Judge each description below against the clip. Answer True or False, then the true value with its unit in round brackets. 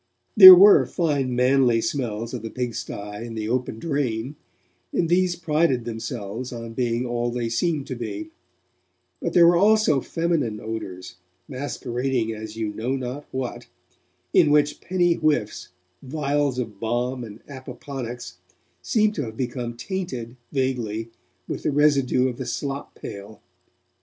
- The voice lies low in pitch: True (125 Hz)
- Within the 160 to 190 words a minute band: False (140 wpm)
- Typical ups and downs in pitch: True (4.2 semitones)